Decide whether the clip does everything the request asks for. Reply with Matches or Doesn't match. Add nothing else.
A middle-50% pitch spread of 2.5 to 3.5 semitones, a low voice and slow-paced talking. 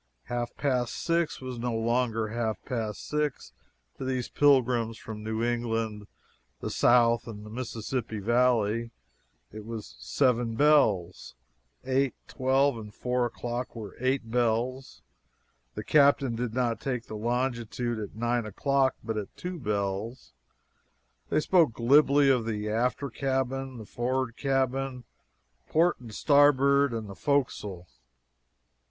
Matches